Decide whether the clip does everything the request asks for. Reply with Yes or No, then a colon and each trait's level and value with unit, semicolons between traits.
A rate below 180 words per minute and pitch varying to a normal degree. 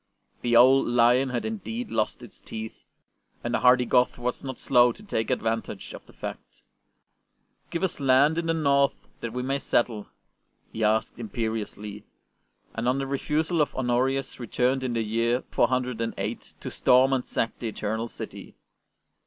Yes: average, 165 wpm; average, 3.0 semitones